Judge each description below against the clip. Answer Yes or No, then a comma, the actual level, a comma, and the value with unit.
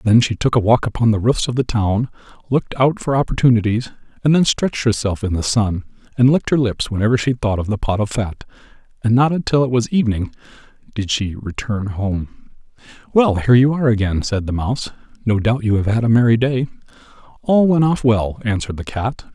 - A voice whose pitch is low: Yes, low, 115 Hz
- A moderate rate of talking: No, fast, 210 wpm